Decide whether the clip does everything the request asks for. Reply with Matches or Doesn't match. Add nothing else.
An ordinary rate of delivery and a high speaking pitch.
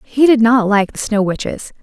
Doesn't match